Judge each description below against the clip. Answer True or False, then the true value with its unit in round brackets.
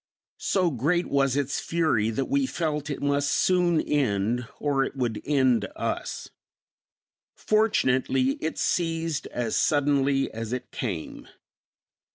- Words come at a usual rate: False (125 wpm)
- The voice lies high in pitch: False (140 Hz)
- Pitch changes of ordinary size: True (4.4 semitones)